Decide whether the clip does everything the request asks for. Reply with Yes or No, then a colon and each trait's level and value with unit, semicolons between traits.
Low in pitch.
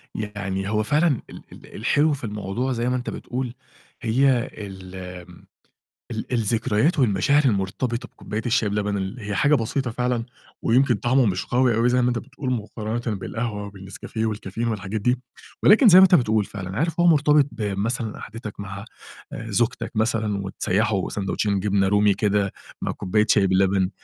Yes: low, 110 Hz